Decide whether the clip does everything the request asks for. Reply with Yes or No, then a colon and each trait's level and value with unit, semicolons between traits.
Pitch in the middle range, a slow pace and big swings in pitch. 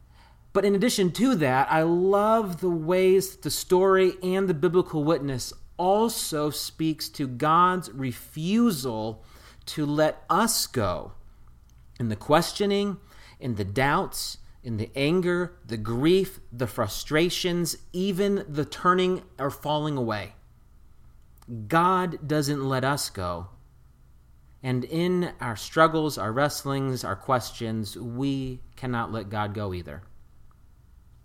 Yes: medium, 145 Hz; slow, 120 wpm; wide, 7.3 semitones